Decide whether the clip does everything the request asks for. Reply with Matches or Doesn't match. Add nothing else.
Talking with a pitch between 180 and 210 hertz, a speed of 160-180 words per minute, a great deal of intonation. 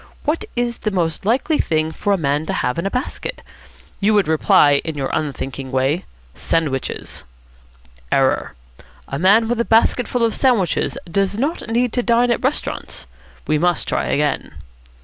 Matches